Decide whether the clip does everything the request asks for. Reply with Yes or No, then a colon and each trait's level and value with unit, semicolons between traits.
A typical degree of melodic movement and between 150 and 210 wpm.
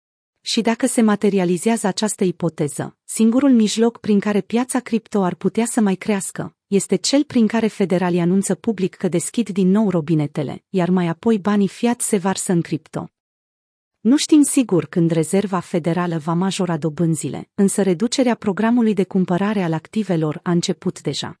Yes: average, 4.0 semitones; average, 160 wpm